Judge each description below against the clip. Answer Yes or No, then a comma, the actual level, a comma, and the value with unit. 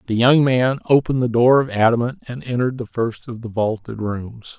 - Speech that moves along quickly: Yes, fast, 210 wpm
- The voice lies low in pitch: Yes, low, 120 Hz